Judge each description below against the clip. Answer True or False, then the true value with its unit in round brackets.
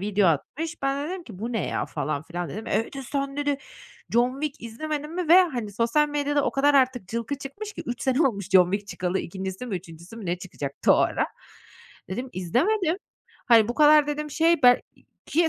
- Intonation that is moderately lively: False (6.9 semitones)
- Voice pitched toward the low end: False (250 Hz)